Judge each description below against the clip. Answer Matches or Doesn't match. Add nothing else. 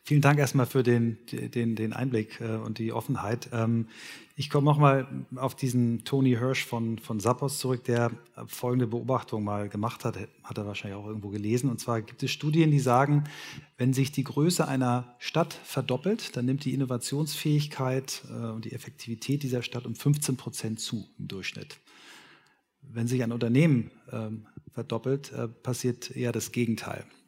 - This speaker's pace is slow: Doesn't match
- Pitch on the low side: Matches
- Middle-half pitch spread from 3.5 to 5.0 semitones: Doesn't match